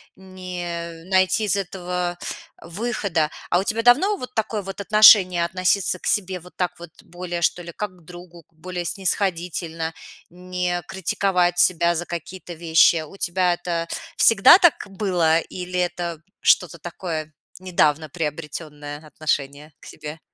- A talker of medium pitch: Yes, medium, 175 Hz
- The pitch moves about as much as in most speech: No, narrow, 2.2 semitones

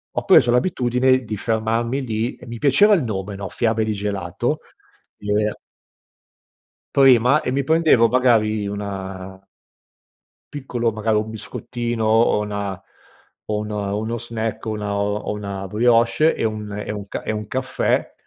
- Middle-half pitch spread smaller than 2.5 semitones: No, average, 2.9 semitones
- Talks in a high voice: No, low, 110 Hz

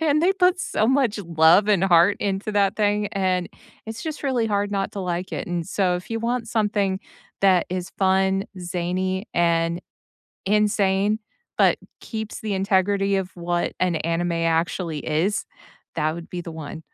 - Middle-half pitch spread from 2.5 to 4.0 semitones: Yes, average, 3.1 semitones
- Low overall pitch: No, high, 190 Hz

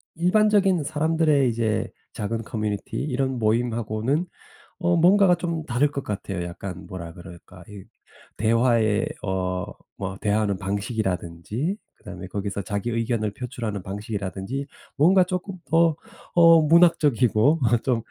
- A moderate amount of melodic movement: No, wide, 7.5 semitones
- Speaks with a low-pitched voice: Yes, low, 115 Hz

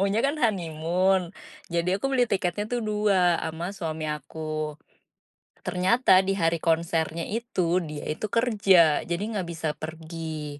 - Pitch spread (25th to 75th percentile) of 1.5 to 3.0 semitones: No, average, 3.7 semitones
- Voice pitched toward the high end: No, medium, 170 Hz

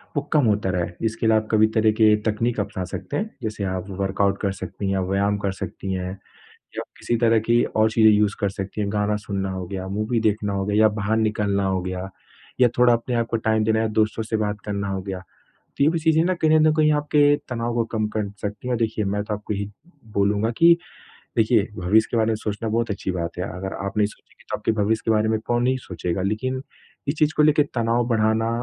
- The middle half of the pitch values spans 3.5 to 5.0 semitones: No, average, 2.7 semitones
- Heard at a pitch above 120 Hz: No, low, 110 Hz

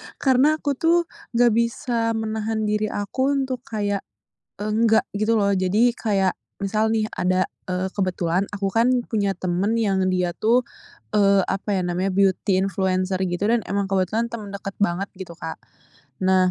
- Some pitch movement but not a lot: Yes, average, 3.2 semitones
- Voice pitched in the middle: No, high, 205 Hz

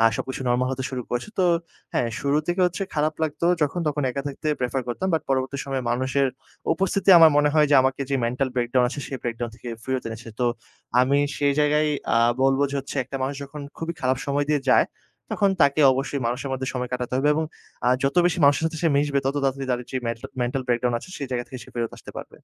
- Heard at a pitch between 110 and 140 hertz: Yes, low, 135 Hz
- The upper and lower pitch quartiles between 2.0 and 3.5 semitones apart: Yes, average, 2.7 semitones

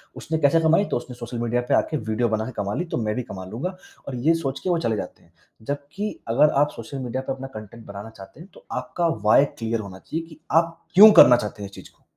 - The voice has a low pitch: Yes, low, 125 Hz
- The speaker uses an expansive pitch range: Yes, wide, 6.4 semitones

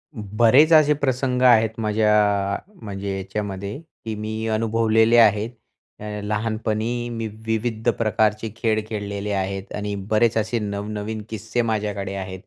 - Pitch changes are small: Yes, narrow, 1.7 semitones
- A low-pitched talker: Yes, low, 110 Hz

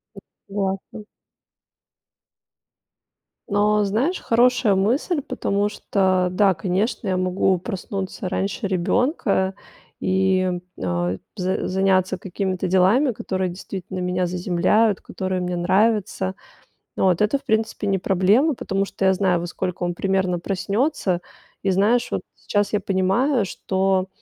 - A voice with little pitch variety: Yes, narrow, 2.2 semitones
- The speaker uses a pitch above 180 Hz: Yes, high, 190 Hz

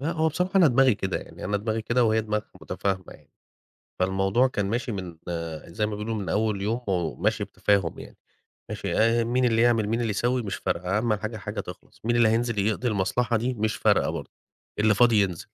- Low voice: Yes, low, 110 Hz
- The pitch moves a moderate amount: Yes, average, 3.0 semitones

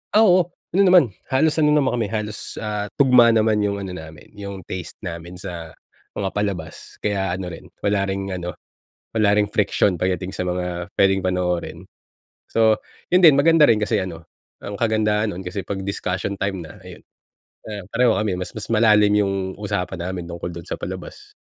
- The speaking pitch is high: No, low, 100 Hz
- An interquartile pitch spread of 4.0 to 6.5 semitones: No, average, 3.1 semitones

